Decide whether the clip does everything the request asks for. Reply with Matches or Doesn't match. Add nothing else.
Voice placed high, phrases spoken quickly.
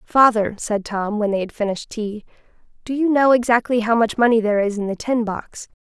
Matches